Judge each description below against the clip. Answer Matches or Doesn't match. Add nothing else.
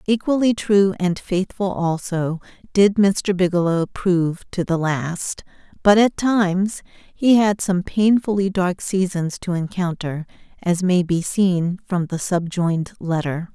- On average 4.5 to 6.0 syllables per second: Doesn't match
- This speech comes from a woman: Matches